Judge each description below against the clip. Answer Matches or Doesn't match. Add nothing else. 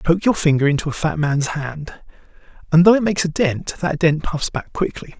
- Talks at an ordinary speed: Doesn't match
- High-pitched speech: Doesn't match